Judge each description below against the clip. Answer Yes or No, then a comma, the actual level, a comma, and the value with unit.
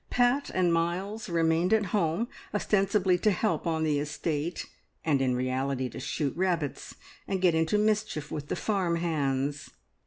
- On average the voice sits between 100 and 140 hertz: No, medium, 170 Hz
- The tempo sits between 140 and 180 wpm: Yes, average, 155 wpm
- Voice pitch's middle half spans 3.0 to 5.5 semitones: Yes, average, 4.9 semitones